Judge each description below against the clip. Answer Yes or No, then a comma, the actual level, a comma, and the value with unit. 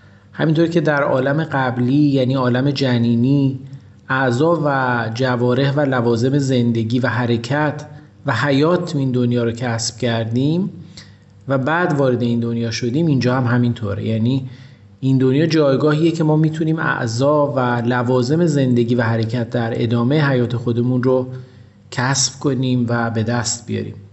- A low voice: Yes, low, 130 Hz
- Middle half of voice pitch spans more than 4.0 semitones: No, average, 3.1 semitones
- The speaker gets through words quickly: No, average, 140 wpm